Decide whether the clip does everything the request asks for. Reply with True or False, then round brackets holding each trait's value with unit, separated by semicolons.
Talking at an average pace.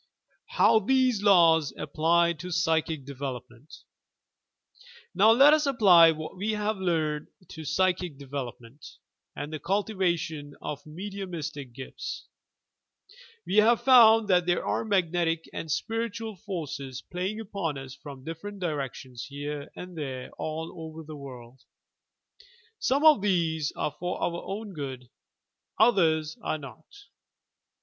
False (125 wpm)